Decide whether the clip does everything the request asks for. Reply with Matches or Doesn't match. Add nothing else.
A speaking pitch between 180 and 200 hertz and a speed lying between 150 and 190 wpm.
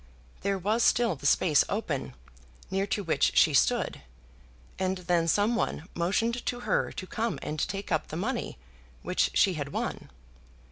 Matches